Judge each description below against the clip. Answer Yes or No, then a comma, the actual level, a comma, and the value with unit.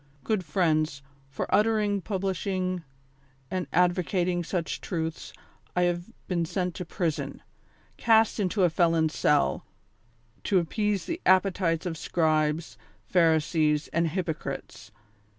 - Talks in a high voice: No, medium, 175 Hz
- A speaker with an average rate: No, slow, 115 wpm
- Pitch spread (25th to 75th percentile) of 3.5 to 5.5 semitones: No, average, 2.9 semitones